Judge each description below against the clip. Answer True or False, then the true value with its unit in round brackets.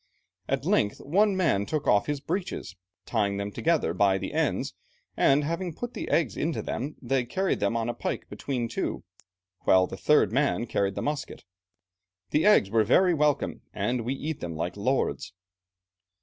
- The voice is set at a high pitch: False (135 Hz)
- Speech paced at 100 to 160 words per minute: False (175 wpm)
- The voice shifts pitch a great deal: True (7.3 semitones)